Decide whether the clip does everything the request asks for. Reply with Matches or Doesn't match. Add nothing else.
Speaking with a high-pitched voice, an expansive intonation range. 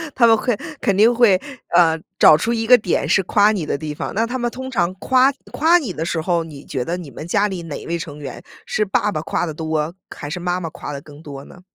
Doesn't match